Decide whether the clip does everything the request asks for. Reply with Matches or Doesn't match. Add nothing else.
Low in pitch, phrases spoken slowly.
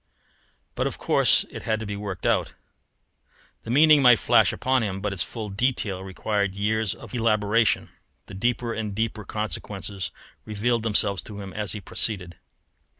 Doesn't match